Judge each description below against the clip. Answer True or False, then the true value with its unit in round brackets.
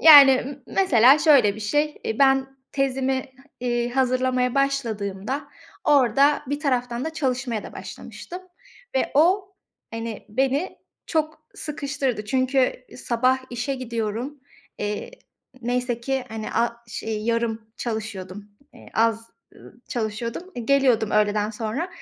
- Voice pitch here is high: True (250 Hz)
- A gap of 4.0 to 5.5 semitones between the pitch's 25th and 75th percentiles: False (3.5 semitones)